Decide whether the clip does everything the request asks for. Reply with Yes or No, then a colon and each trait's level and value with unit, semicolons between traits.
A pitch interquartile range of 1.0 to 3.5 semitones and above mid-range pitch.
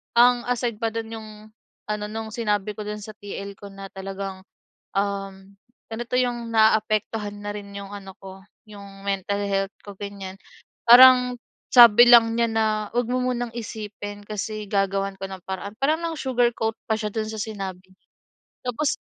Yes: average, 2.8 semitones; high, 210 Hz